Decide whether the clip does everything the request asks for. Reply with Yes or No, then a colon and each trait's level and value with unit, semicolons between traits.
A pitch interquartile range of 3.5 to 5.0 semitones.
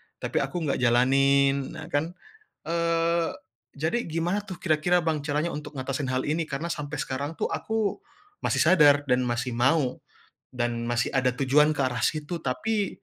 Yes: average, 4.3 semitones